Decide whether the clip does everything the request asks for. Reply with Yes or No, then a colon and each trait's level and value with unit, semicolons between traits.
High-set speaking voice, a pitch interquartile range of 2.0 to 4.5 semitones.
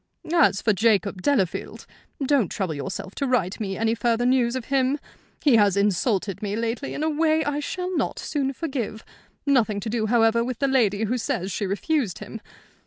No: high, 230 Hz; average, 4.9 semitones